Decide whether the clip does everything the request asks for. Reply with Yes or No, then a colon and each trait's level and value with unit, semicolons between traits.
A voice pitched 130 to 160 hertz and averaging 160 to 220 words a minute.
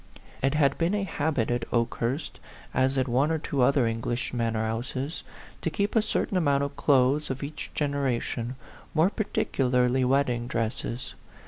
Yes: low, 135 Hz; average, 175 wpm